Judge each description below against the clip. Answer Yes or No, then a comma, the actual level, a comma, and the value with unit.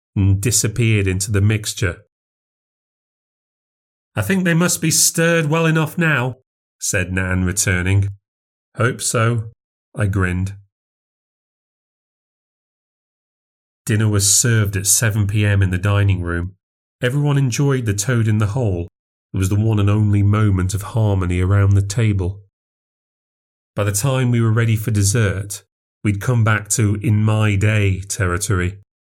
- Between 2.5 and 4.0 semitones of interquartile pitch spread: Yes, average, 3.2 semitones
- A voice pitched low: Yes, low, 100 Hz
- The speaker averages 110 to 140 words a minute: Yes, slow, 135 wpm